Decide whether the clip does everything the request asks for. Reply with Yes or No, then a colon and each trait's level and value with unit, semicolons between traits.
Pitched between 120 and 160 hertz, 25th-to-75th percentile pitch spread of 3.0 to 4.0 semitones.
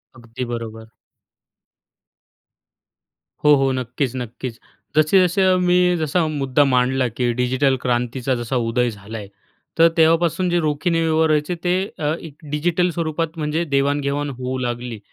No: medium, 140 Hz; average, 4.6 semitones